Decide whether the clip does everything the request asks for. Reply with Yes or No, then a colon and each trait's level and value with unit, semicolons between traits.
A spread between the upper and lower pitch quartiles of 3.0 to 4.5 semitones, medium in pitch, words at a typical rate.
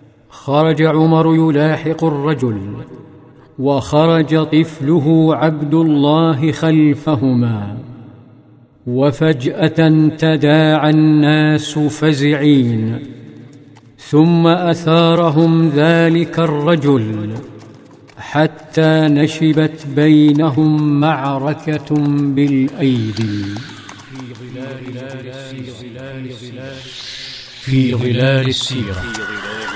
No: average, 3.3 semitones; medium, 150 Hz; slow, 50 wpm